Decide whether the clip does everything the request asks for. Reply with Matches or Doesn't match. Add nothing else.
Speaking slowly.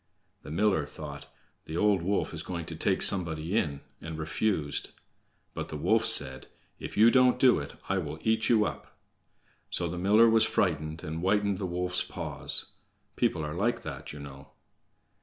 Doesn't match